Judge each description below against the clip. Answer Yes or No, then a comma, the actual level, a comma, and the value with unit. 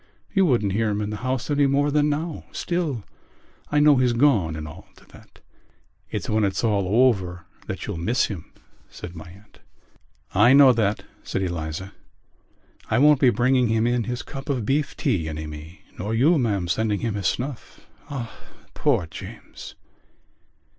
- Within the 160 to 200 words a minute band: Yes, average, 175 wpm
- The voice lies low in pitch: Yes, low, 115 Hz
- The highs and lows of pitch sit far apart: Yes, wide, 5.9 semitones